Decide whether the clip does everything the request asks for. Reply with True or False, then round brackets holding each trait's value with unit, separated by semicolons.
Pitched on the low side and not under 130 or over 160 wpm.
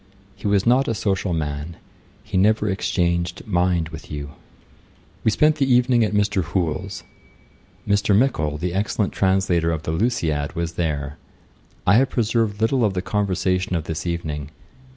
True (95 Hz; 155 wpm)